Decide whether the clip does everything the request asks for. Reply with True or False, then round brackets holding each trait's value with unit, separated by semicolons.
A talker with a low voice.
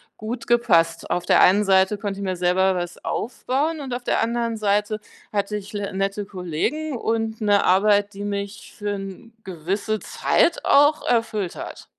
False (205 Hz)